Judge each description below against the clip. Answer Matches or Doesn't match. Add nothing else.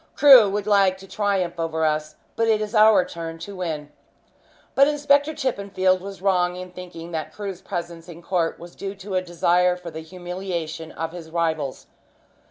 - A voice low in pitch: Doesn't match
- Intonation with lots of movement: Doesn't match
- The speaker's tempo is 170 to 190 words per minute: Matches